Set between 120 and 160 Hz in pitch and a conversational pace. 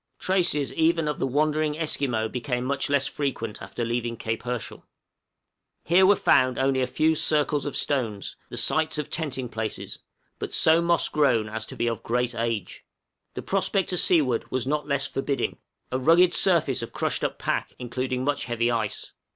Yes: low, 135 Hz; average, 175 wpm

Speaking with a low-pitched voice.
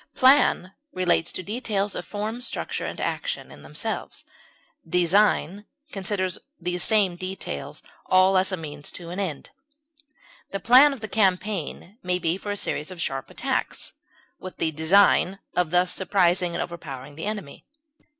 No: medium, 185 Hz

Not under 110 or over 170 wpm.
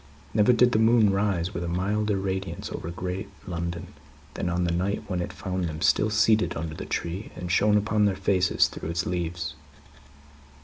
No: average, 185 wpm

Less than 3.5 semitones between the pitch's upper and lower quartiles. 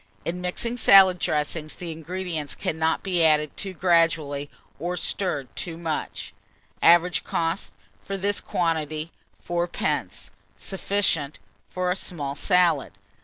Yes: average, 3.0 semitones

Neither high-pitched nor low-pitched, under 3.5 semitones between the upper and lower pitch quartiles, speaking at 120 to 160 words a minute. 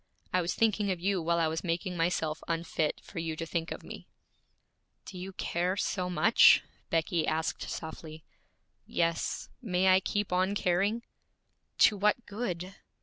Yes: medium, 180 Hz; average, 2.8 semitones; average, 155 wpm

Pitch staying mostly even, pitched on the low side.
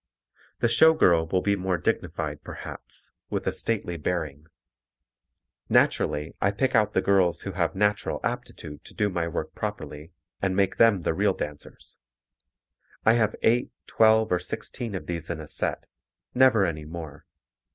No: average, 4.3 semitones; very low, 95 Hz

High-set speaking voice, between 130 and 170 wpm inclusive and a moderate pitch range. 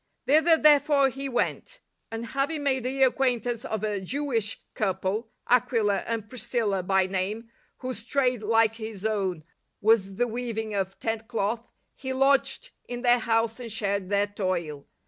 Yes: high, 225 Hz; average, 150 wpm; average, 3.9 semitones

